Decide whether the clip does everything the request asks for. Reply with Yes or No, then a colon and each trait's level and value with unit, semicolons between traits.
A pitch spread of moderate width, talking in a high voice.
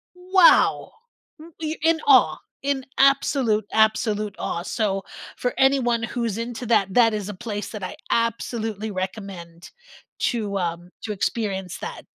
Yes: average, 3.9 semitones; high, 220 Hz